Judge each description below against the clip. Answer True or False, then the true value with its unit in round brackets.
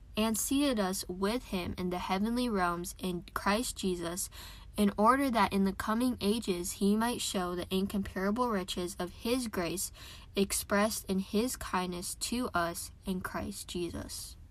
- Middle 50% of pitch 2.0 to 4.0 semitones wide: True (3.5 semitones)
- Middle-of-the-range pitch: False (195 Hz)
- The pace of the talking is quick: False (155 wpm)